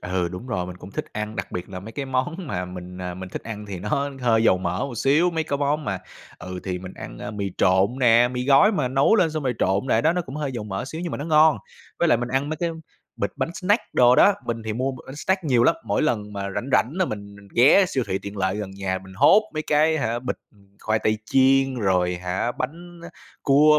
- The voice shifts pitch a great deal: Yes, wide, 7.0 semitones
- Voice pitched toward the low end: Yes, low, 120 Hz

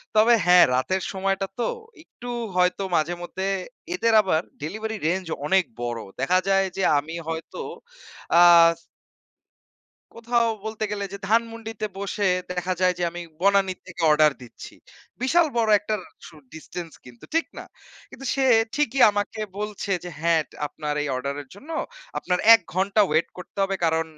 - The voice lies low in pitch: No, high, 190 Hz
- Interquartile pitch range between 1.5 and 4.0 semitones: No, average, 4.6 semitones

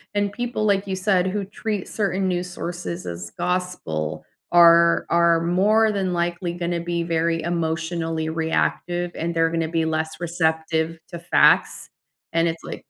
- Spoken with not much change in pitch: Yes, narrow, 2.0 semitones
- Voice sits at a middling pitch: Yes, medium, 170 Hz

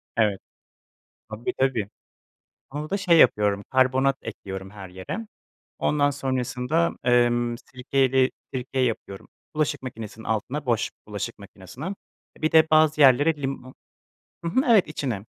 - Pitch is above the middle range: No, low, 130 Hz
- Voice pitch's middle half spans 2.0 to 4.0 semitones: No, average, 4.8 semitones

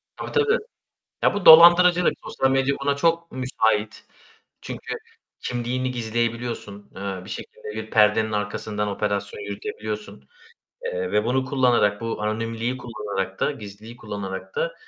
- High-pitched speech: No, low, 110 Hz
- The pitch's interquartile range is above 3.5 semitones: Yes, average, 4.0 semitones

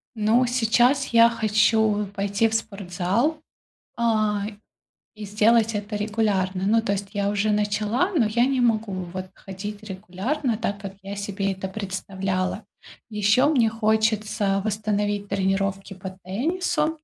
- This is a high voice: Yes, high, 210 Hz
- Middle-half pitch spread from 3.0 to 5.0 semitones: No, narrow, 2.4 semitones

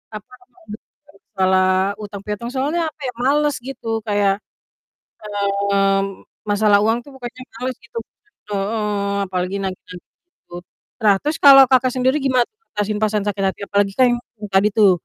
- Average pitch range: Yes, average, 4.3 semitones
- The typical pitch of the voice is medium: No, high, 210 Hz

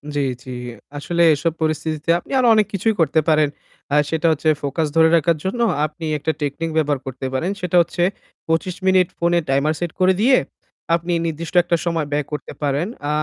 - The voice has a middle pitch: Yes, medium, 160 Hz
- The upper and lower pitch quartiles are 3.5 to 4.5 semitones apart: No, narrow, 2.6 semitones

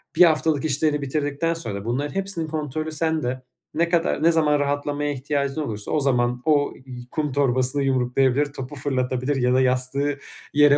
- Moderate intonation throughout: Yes, average, 3.1 semitones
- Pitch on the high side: No, medium, 145 Hz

